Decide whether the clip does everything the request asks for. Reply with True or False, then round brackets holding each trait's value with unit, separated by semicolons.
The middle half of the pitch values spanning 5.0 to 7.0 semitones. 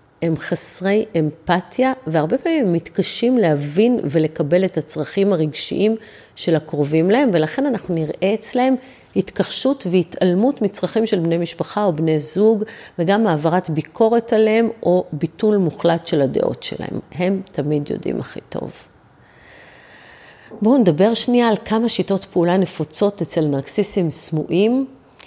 True (5.3 semitones)